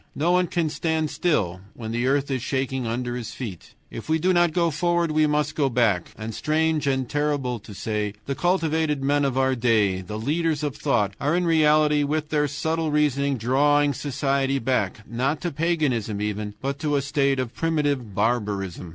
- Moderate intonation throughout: Yes, average, 4.6 semitones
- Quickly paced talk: No, average, 190 wpm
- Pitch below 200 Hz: Yes, medium, 140 Hz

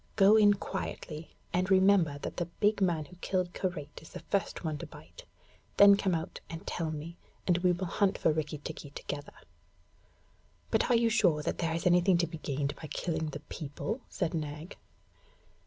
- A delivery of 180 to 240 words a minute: Yes, average, 190 wpm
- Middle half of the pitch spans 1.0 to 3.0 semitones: No, average, 3.6 semitones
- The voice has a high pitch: No, medium, 170 Hz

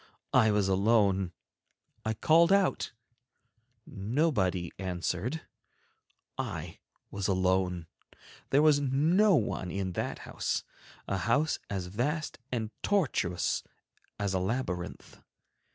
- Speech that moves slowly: Yes, slow, 100 wpm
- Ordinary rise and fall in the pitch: No, wide, 7.3 semitones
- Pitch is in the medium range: No, low, 105 Hz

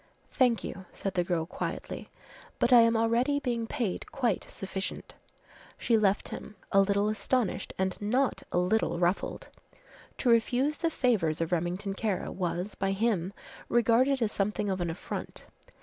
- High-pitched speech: Yes, high, 210 Hz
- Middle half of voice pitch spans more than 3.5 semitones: Yes, average, 4.0 semitones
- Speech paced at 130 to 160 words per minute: Yes, average, 155 wpm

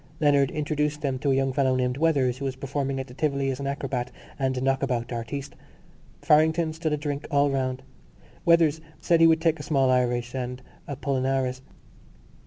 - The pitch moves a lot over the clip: No, narrow, 2.4 semitones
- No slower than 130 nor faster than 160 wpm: No, average, 180 wpm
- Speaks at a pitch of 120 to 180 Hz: Yes, low, 135 Hz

